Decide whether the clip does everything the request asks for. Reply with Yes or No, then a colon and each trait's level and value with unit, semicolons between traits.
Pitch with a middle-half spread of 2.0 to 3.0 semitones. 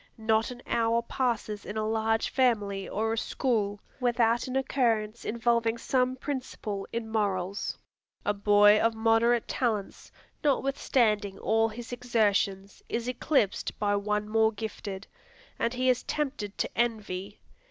Yes: narrow, 2.6 semitones